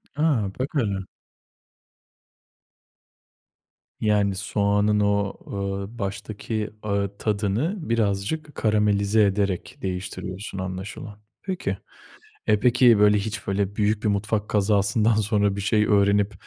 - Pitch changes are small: Yes, narrow, 1.6 semitones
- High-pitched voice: No, low, 105 Hz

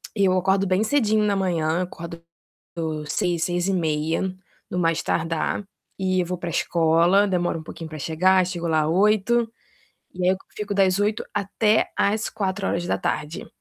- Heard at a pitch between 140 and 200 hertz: Yes, medium, 185 Hz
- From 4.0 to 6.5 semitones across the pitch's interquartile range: No, average, 3.1 semitones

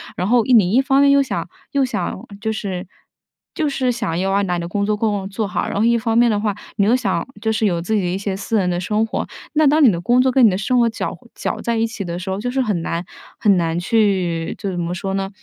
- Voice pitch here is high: Yes, high, 210 Hz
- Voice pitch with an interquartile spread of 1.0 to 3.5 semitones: No, average, 4.2 semitones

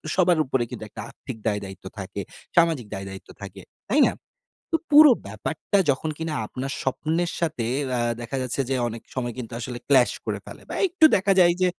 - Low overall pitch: Yes, low, 130 Hz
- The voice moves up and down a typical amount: No, wide, 7.1 semitones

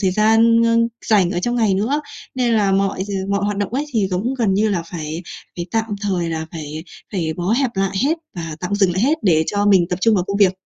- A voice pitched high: Yes, high, 200 Hz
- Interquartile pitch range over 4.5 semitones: No, average, 3.9 semitones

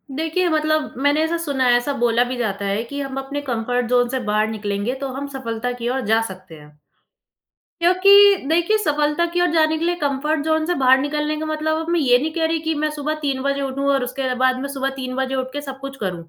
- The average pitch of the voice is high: Yes, very high, 275 Hz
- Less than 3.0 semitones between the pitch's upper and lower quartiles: No, average, 4.0 semitones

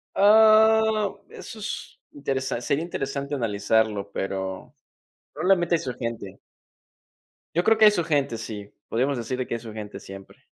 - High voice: No, low, 135 Hz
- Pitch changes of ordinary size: No, wide, 8.9 semitones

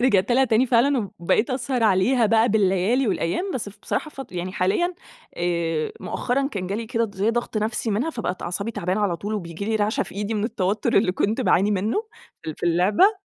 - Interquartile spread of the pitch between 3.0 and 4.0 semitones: No, average, 4.4 semitones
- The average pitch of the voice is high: Yes, high, 210 Hz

